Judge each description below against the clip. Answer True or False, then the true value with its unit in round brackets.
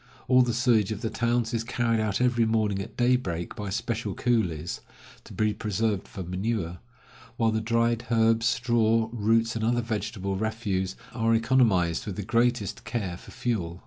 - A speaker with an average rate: True (170 wpm)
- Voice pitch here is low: True (110 Hz)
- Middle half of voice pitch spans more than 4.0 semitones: False (2.7 semitones)